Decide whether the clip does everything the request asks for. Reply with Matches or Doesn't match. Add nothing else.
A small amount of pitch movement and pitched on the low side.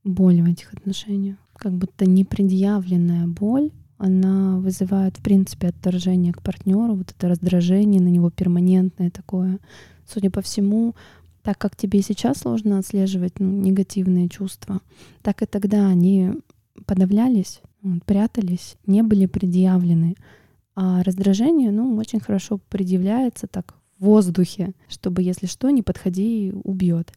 Doesn't match